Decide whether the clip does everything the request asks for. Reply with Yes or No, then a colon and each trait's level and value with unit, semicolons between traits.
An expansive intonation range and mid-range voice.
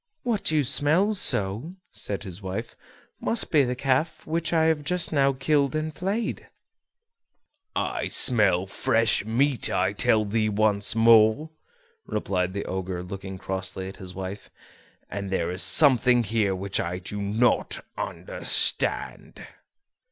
No: wide, 7.5 semitones; low, 115 Hz